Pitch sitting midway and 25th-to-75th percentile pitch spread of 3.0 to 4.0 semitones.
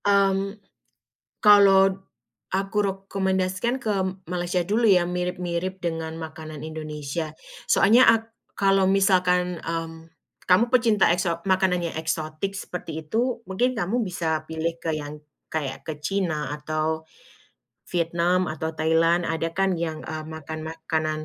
Yes: medium, 175 Hz; average, 3.4 semitones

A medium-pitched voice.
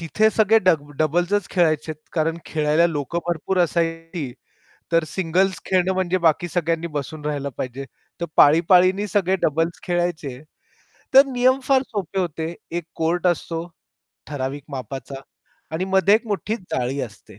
Yes: medium, 170 Hz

